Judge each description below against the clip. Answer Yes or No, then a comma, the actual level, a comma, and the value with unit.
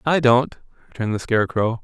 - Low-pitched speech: Yes, low, 120 Hz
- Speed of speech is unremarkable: Yes, average, 165 wpm